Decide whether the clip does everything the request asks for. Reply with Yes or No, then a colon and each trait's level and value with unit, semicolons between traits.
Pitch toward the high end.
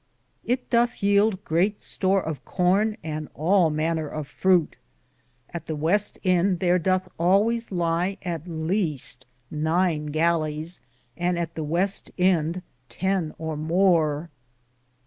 No: medium, 175 Hz